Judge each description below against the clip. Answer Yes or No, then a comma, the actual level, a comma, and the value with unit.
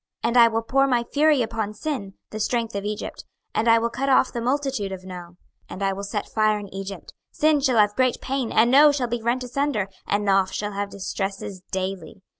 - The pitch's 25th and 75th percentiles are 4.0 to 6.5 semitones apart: Yes, average, 4.4 semitones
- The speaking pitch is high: Yes, high, 220 Hz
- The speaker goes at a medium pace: No, fast, 225 wpm